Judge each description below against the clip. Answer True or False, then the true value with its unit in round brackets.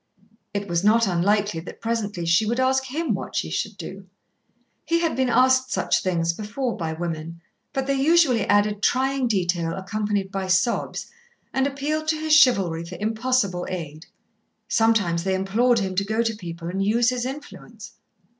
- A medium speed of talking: True (170 wpm)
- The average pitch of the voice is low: False (210 Hz)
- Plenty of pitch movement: True (5.8 semitones)